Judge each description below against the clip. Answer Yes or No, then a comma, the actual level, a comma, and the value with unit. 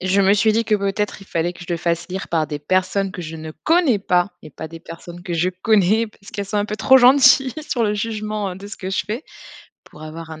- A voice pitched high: Yes, high, 195 Hz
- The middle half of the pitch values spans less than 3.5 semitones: No, average, 3.8 semitones